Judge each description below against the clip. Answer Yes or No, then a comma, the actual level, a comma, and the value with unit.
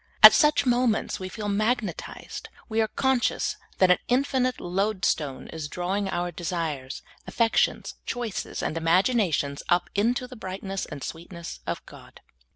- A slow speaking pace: No, average, 155 wpm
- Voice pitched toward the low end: No, high, 195 Hz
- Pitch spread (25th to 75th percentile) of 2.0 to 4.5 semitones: No, wide, 5.5 semitones